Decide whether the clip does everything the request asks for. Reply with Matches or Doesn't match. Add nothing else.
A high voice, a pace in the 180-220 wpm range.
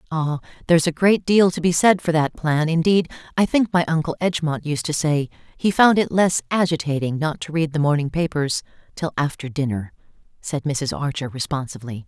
Doesn't match